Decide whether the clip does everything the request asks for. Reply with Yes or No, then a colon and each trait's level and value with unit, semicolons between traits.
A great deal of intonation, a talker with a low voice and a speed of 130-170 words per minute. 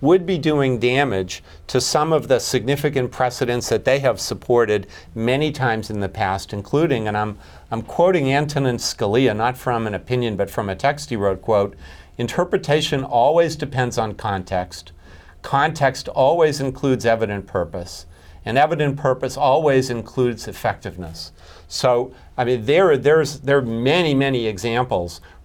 Yes: wide, 5.9 semitones; low, 120 Hz; average, 150 wpm